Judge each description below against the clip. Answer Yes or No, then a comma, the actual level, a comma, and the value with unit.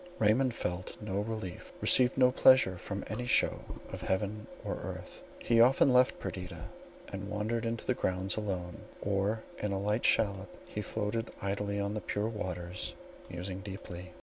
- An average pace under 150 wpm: No, average, 160 wpm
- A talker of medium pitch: No, low, 105 Hz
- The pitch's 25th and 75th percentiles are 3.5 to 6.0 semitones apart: No, average, 3.0 semitones